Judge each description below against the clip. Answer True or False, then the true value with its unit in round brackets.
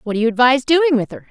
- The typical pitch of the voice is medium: False (250 Hz)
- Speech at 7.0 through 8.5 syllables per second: True (7.5 syllables/s)